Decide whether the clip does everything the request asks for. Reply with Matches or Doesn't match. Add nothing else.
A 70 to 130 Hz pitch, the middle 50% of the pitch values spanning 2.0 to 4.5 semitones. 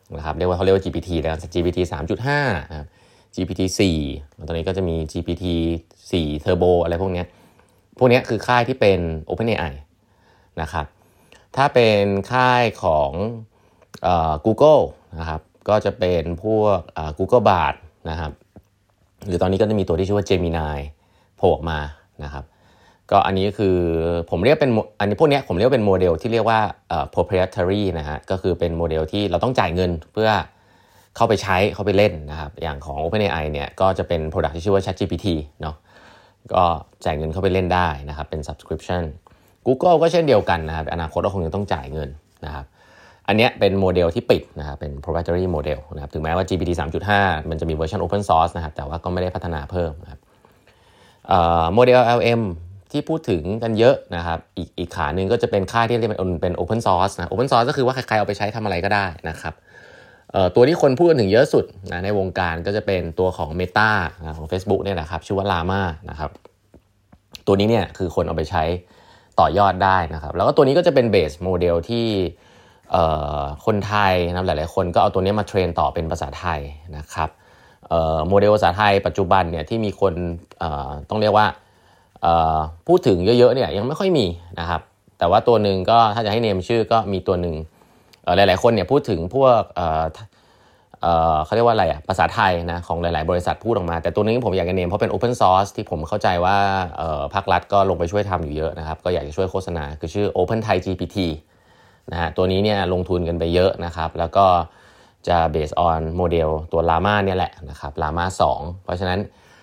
Matches